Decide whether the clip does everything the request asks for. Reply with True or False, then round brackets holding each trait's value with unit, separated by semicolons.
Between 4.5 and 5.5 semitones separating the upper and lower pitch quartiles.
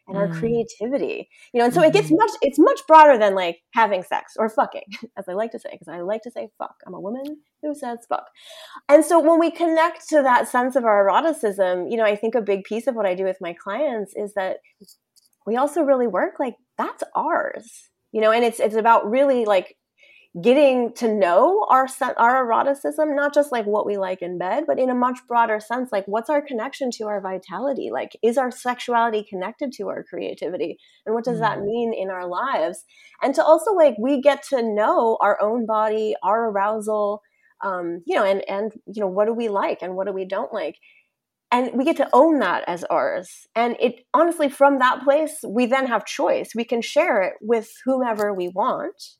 True (5.2 semitones)